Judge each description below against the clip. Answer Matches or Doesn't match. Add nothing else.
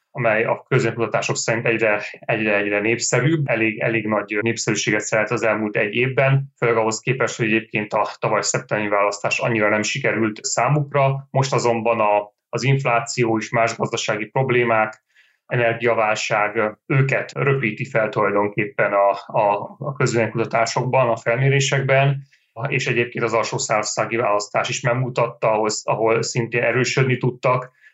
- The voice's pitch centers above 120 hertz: Doesn't match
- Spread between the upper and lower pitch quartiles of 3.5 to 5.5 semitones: Doesn't match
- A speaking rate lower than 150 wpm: Matches